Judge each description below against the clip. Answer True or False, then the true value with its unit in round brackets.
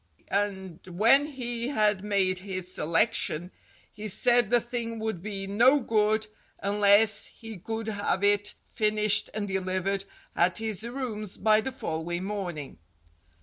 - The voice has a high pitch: True (210 Hz)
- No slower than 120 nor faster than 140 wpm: True (135 wpm)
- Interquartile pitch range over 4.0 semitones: False (2.9 semitones)